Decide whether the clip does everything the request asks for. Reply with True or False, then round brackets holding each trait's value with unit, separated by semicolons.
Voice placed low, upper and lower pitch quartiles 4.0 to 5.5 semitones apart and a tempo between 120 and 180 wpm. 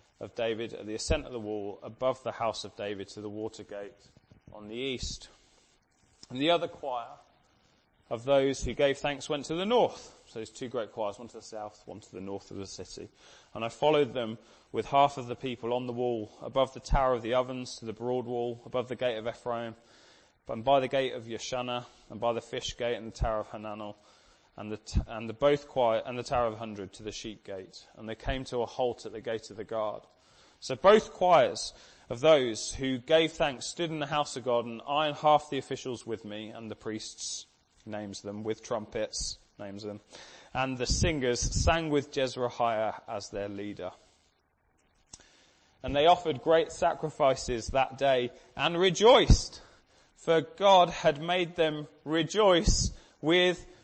False (120 Hz; 4.7 semitones; 195 wpm)